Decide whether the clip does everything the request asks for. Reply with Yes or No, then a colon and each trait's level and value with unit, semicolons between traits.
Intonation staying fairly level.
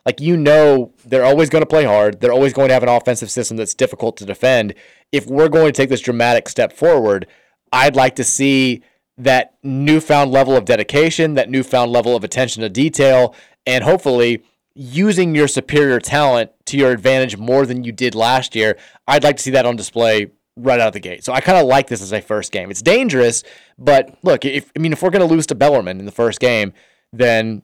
No: average, 3.3 semitones